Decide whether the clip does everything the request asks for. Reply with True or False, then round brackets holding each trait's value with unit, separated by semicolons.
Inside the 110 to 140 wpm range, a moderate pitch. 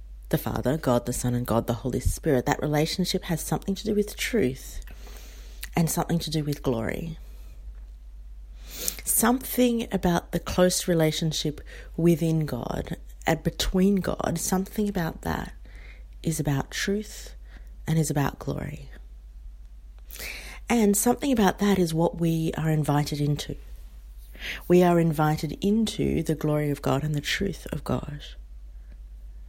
True (135 wpm; 150 Hz)